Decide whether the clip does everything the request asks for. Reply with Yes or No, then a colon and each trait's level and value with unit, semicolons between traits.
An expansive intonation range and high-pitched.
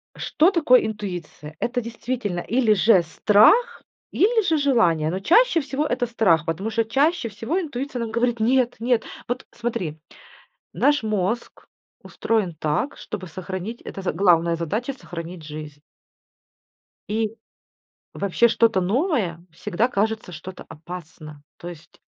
Yes: wide, 6.0 semitones; high, 215 Hz